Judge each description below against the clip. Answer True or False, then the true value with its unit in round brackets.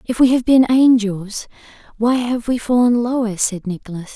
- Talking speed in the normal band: True (175 wpm)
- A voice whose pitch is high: True (230 Hz)